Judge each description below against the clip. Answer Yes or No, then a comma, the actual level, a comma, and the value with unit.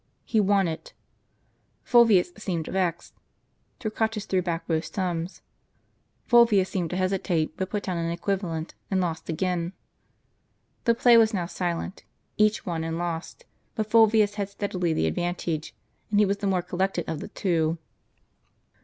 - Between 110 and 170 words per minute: Yes, average, 150 wpm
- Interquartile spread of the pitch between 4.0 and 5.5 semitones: No, average, 3.5 semitones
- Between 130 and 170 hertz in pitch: No, medium, 185 Hz